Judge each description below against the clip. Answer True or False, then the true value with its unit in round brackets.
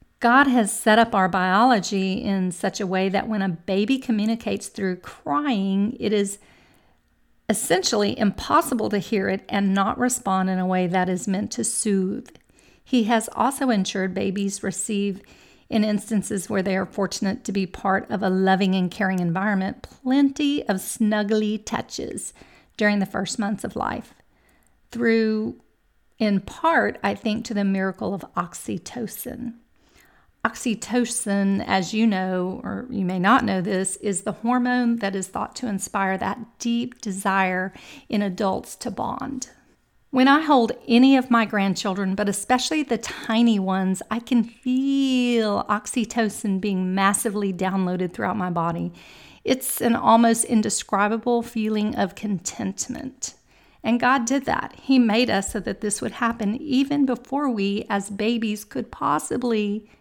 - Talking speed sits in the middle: True (150 wpm)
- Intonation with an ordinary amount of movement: True (3.6 semitones)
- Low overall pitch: False (210 Hz)